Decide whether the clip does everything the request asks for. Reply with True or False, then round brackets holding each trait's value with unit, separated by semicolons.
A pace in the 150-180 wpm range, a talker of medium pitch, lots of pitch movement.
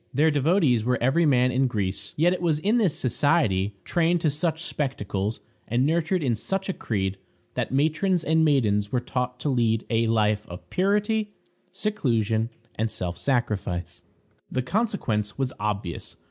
False (160 wpm; 130 Hz; 7.4 semitones)